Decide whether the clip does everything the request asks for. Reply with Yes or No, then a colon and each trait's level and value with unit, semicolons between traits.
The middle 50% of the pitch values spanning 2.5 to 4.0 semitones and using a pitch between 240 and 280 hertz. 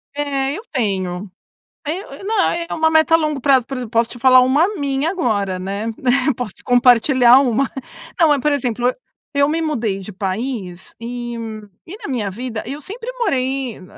No: average, 4.5 semitones; very high, 255 Hz